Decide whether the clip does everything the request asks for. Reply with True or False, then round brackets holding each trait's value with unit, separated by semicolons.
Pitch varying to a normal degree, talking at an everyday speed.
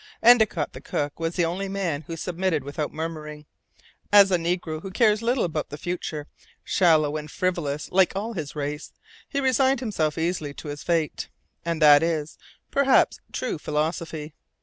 True (4.1 semitones; 165 wpm)